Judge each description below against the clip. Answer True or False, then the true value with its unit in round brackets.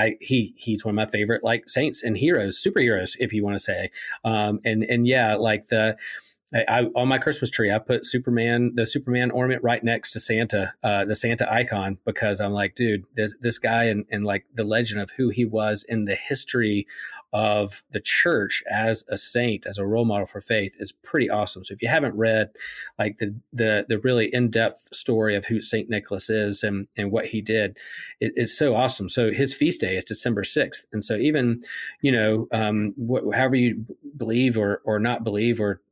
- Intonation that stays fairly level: True (2.3 semitones)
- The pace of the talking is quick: True (210 wpm)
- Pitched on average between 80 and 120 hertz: True (110 Hz)